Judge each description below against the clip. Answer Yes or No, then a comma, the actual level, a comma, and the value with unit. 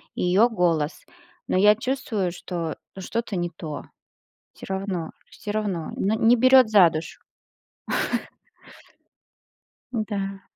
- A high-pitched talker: Yes, high, 195 Hz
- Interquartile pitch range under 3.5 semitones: No, average, 4.0 semitones